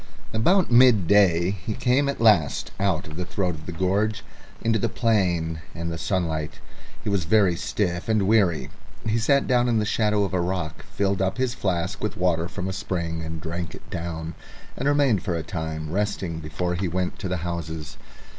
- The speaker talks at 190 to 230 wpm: Yes, average, 195 wpm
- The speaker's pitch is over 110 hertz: No, very low, 95 Hz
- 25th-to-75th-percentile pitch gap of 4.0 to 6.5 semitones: Yes, average, 4.4 semitones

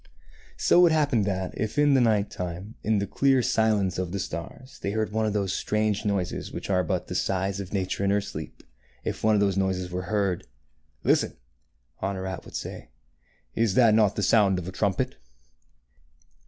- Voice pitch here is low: Yes, low, 100 Hz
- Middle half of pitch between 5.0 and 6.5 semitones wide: No, average, 2.7 semitones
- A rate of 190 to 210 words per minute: Yes, average, 200 wpm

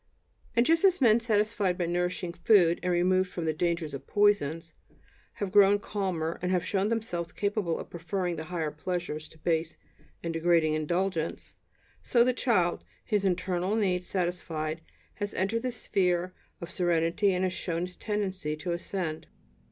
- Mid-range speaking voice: Yes, medium, 180 Hz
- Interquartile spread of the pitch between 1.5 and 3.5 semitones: Yes, average, 3.2 semitones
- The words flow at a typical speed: Yes, average, 160 wpm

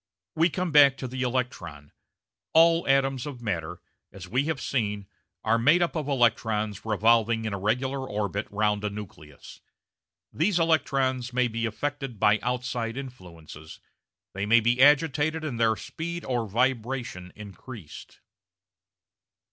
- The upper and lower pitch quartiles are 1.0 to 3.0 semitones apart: No, average, 4.6 semitones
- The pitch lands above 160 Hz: No, low, 120 Hz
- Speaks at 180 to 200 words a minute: No, average, 140 wpm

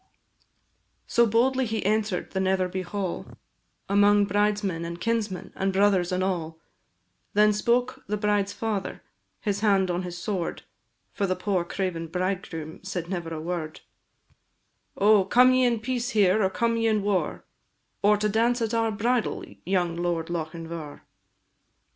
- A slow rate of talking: No, average, 150 wpm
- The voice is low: No, high, 200 Hz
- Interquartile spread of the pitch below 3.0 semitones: No, average, 3.4 semitones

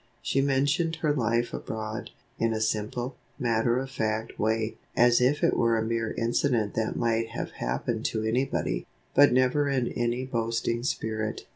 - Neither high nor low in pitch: No, low, 115 Hz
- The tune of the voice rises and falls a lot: No, narrow, 2.6 semitones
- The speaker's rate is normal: Yes, average, 160 wpm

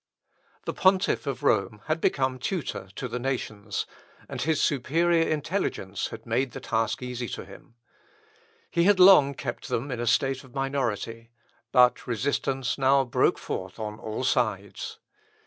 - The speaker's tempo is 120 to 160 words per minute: Yes, average, 150 wpm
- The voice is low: Yes, low, 130 Hz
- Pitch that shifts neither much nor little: Yes, average, 3.7 semitones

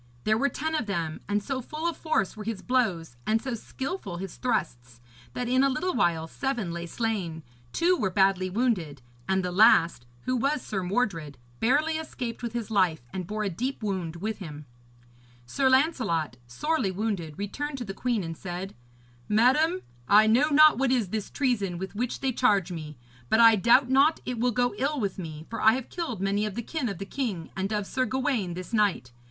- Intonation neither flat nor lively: No, wide, 5.9 semitones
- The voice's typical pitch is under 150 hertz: No, high, 215 Hz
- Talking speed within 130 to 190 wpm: No, fast, 205 wpm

